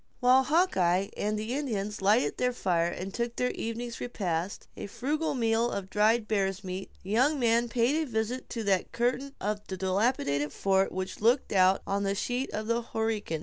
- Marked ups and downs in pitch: No, average, 4.0 semitones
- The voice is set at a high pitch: Yes, high, 220 Hz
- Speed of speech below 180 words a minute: No, average, 190 wpm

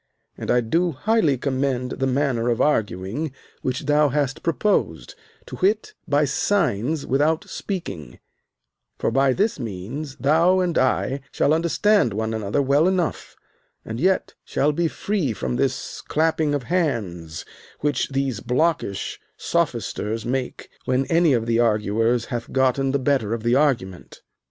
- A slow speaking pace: No, average, 145 wpm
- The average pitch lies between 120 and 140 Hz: Yes, low, 135 Hz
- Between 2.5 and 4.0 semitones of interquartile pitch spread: No, average, 5.3 semitones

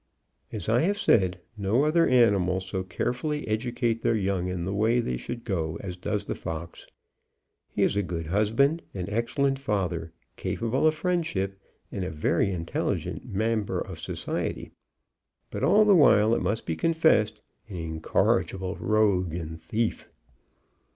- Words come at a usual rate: Yes, average, 150 wpm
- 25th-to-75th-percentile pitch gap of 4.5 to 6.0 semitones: Yes, average, 4.8 semitones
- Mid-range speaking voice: No, low, 105 Hz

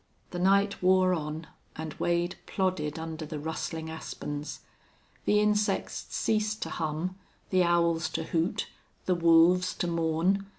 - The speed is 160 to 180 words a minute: No, slow, 135 wpm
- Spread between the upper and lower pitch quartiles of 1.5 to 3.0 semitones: Yes, average, 2.7 semitones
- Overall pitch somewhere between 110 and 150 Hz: No, medium, 170 Hz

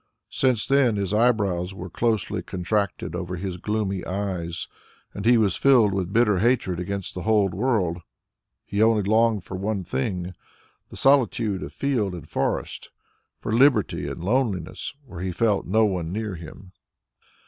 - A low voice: Yes, low, 100 Hz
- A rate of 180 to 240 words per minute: No, average, 155 wpm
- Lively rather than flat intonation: No, average, 3.7 semitones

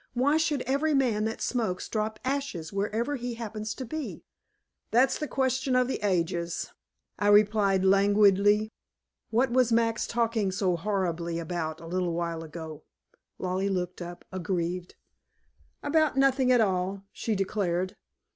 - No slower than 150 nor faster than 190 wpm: No, average, 140 wpm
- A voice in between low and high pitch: No, high, 205 Hz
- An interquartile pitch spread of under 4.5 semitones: No, average, 5.3 semitones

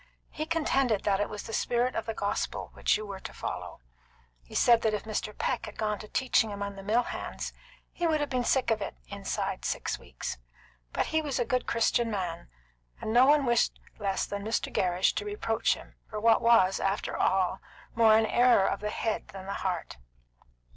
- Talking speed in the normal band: No, fast, 210 wpm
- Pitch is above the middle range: Yes, high, 220 Hz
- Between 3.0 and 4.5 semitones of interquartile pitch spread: Yes, average, 3.5 semitones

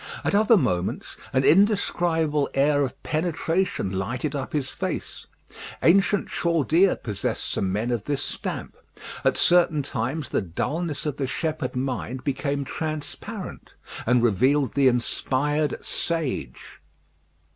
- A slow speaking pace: Yes, slow, 125 wpm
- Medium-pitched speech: Yes, medium, 145 Hz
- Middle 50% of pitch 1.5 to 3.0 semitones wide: No, average, 4.3 semitones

